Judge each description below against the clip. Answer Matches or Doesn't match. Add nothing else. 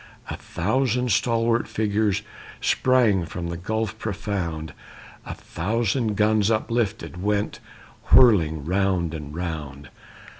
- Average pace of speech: Doesn't match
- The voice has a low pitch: Matches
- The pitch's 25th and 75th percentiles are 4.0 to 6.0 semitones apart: Matches